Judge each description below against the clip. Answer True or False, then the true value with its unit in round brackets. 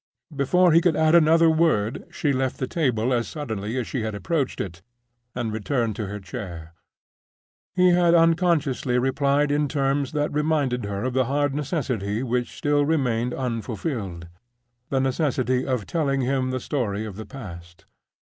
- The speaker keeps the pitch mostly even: False (4.8 semitones)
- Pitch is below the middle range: True (130 Hz)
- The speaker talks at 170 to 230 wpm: False (155 wpm)